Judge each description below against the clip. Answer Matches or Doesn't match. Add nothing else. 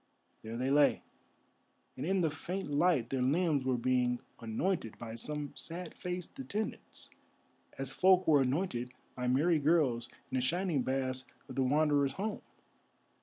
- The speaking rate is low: Doesn't match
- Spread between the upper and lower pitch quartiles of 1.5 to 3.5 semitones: Doesn't match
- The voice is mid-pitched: Matches